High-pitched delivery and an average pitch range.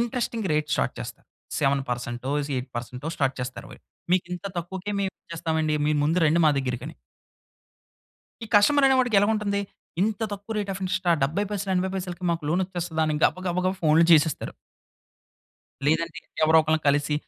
No: medium, 170 Hz; average, 4.5 semitones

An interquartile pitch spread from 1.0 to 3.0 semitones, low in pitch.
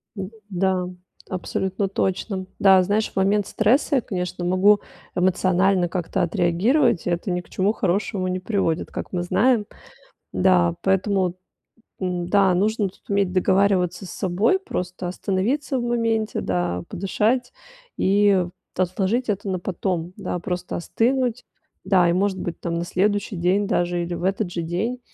No: narrow, 2.4 semitones; high, 190 Hz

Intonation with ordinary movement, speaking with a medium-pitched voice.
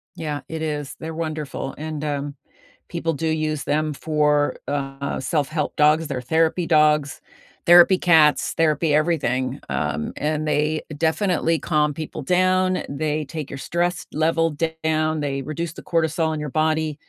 No: narrow, 1.6 semitones; medium, 155 Hz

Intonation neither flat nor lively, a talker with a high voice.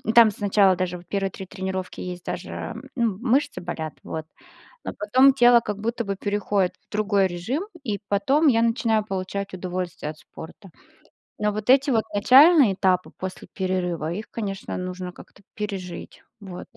Yes: average, 3.7 semitones; high, 200 Hz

